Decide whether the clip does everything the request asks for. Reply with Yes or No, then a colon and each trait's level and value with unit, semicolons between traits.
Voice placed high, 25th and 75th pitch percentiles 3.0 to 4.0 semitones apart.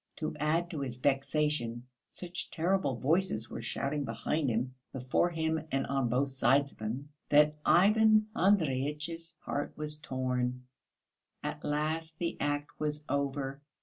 No: medium, 145 Hz; average, 3.4 semitones